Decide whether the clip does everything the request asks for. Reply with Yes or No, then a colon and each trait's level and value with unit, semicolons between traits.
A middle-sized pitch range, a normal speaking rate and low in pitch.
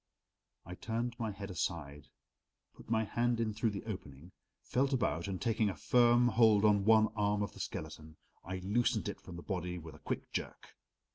Yes: average, 4.4 semitones; average, 190 wpm; low, 105 Hz